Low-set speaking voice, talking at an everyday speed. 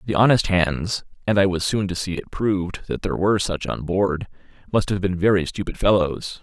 Yes: very low, 95 Hz; average, 195 wpm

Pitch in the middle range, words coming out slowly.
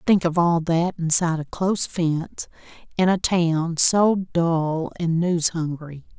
No: medium, 170 Hz; average, 155 wpm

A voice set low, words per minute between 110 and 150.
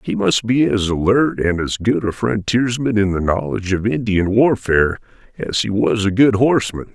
No: low, 105 Hz; average, 190 wpm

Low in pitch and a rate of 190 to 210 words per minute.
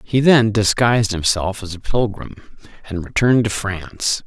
No: low, 105 Hz; average, 155 wpm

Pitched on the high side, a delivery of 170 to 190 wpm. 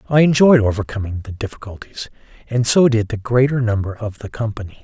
No: low, 110 Hz; average, 175 wpm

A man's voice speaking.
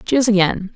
No: female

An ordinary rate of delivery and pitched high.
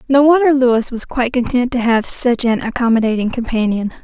Yes: average, 180 wpm; high, 245 Hz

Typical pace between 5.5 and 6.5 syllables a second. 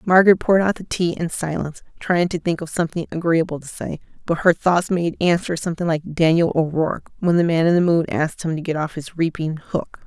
Yes: 6.0 syllables/s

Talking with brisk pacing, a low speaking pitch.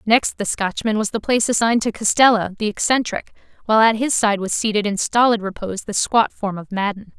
No: fast, 210 wpm; high, 215 Hz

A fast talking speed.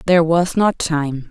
No: average, 185 wpm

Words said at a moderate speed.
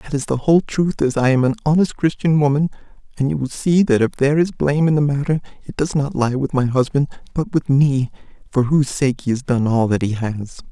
No: fast, 245 wpm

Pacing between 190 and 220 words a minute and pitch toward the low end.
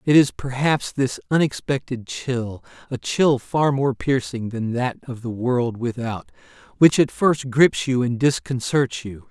No: average, 160 wpm; low, 130 Hz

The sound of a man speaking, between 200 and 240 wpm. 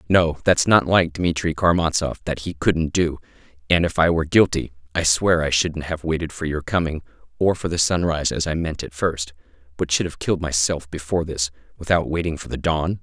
Yes: male; fast, 205 wpm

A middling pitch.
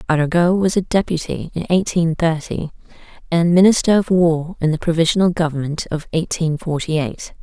Yes: medium, 165 Hz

